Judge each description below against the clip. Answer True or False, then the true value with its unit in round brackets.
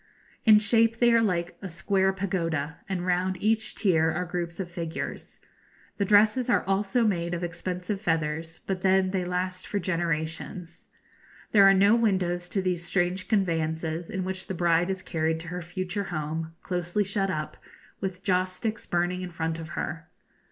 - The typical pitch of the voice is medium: True (180 Hz)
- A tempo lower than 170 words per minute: False (175 wpm)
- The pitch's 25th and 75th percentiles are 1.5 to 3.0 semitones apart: True (2.5 semitones)